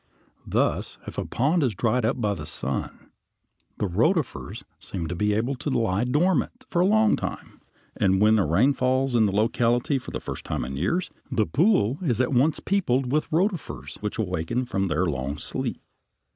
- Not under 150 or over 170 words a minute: No, average, 185 wpm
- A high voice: No, low, 120 Hz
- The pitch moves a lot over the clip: Yes, wide, 7.0 semitones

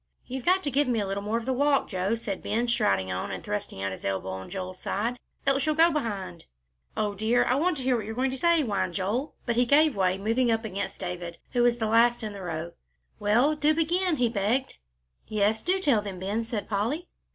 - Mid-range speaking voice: No, high, 225 Hz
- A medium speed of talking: No, fast, 235 wpm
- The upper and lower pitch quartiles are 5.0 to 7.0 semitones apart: Yes, wide, 5.4 semitones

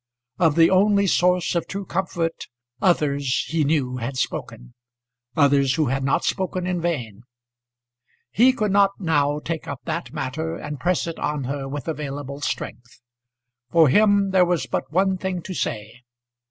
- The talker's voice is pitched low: No, medium, 160 Hz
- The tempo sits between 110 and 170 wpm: Yes, average, 160 wpm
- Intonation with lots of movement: No, average, 4.7 semitones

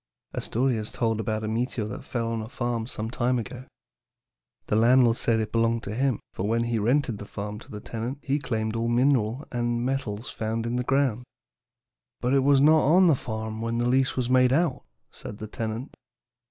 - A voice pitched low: Yes, low, 120 Hz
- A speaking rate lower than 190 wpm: No, fast, 205 wpm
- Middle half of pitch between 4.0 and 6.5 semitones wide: No, narrow, 2.6 semitones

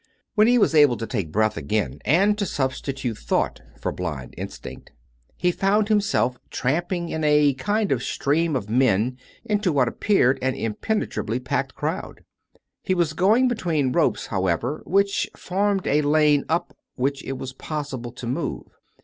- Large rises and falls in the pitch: Yes, wide, 6.7 semitones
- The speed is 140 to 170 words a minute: Yes, average, 165 wpm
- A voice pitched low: No, medium, 145 Hz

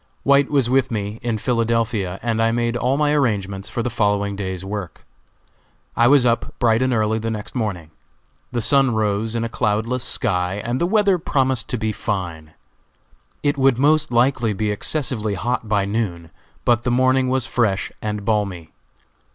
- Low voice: Yes, low, 115 Hz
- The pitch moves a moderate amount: Yes, average, 3.7 semitones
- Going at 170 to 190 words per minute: Yes, average, 175 wpm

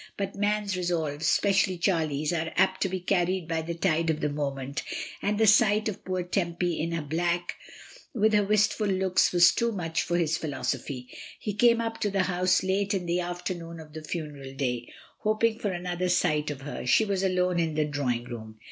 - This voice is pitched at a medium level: Yes, medium, 175 Hz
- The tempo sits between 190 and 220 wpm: Yes, average, 200 wpm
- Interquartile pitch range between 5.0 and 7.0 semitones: No, average, 3.9 semitones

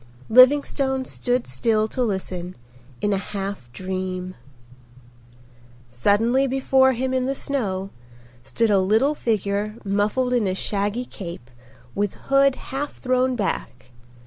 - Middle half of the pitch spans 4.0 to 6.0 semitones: Yes, average, 5.2 semitones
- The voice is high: Yes, high, 215 Hz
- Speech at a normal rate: No, slow, 120 wpm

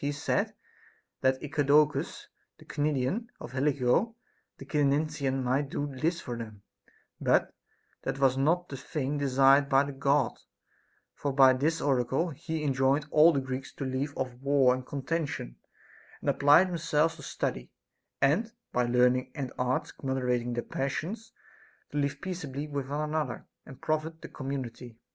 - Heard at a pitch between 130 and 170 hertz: Yes, medium, 140 Hz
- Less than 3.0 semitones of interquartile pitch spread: Yes, narrow, 2.5 semitones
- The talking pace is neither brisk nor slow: Yes, average, 155 wpm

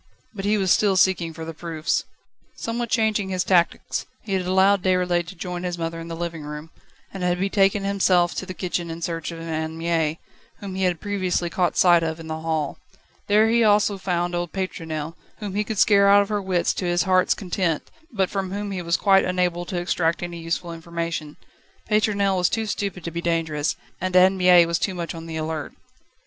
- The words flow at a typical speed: No, fast, 210 wpm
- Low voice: No, medium, 180 Hz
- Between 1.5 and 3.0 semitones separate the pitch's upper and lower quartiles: Yes, narrow, 2.6 semitones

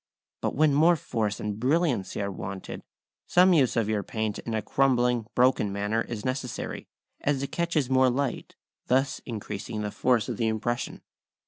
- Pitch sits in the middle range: No, low, 120 Hz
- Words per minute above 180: No, average, 165 wpm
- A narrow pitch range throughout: No, average, 4.1 semitones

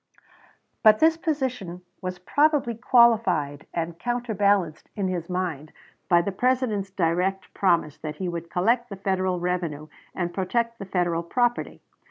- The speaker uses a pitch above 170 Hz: Yes, high, 190 Hz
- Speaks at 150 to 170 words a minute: No, average, 140 wpm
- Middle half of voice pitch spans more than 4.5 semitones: Yes, average, 5.3 semitones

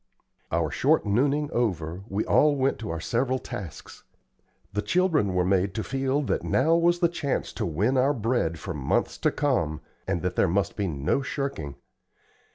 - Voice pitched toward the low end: Yes, low, 115 Hz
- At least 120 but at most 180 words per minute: Yes, average, 175 wpm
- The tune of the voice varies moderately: No, wide, 7.6 semitones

